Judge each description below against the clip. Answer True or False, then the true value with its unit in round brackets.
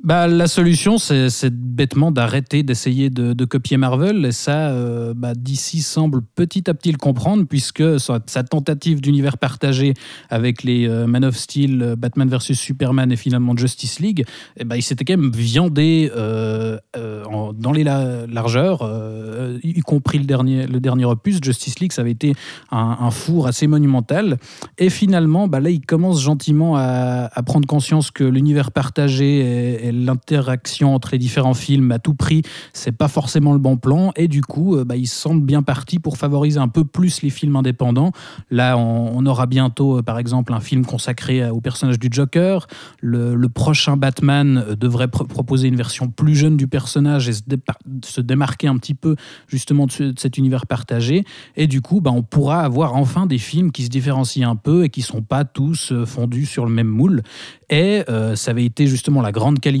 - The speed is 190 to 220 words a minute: True (195 wpm)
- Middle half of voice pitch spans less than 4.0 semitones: True (3.3 semitones)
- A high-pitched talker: False (135 Hz)